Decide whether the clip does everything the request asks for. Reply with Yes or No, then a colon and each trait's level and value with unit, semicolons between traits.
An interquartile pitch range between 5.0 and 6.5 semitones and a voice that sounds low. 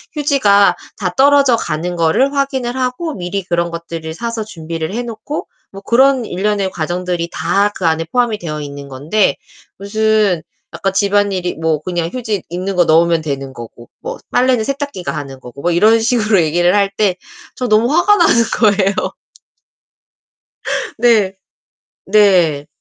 No: wide, 5.5 semitones; high, 195 Hz